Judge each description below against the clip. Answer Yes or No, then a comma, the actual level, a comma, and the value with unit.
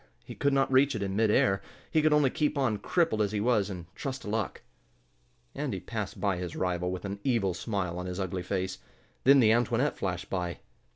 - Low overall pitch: Yes, low, 100 Hz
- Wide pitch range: Yes, wide, 5.9 semitones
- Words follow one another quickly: Yes, fast, 215 wpm